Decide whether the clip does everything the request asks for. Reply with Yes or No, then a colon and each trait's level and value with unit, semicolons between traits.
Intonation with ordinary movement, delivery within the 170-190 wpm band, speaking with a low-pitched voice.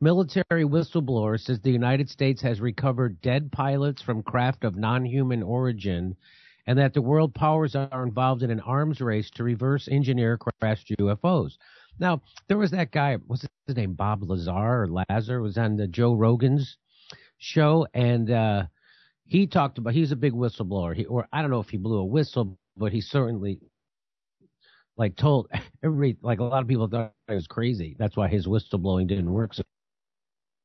Yes: average, 4.3 semitones; average, 175 wpm; low, 120 Hz